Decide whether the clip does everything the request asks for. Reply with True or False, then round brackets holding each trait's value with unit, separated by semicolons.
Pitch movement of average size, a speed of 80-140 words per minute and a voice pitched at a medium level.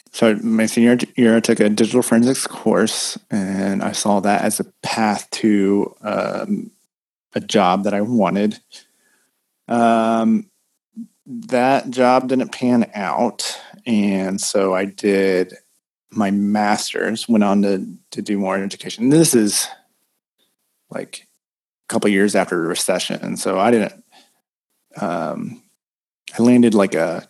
False (3.4 semitones; 135 wpm; 110 Hz)